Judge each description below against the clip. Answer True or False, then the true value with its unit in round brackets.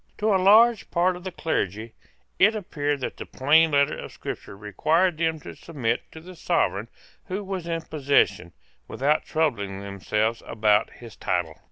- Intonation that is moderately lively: False (8.4 semitones)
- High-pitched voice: False (150 Hz)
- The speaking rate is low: False (165 wpm)